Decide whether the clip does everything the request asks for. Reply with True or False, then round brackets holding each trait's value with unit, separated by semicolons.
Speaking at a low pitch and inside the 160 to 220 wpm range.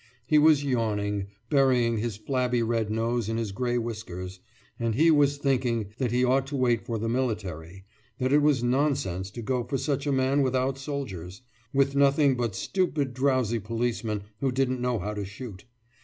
True (125 Hz; 180 wpm)